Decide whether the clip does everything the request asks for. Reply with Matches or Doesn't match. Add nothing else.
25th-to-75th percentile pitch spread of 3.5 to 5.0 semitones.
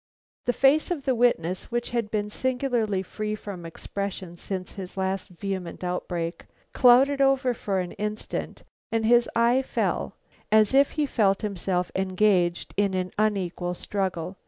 Matches